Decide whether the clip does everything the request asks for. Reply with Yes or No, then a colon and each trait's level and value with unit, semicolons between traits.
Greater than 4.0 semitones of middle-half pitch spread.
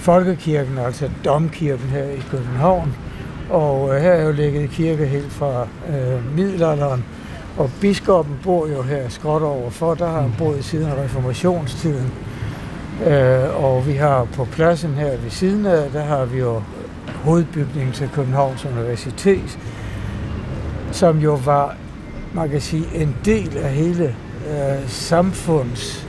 No: average, 3.7 semitones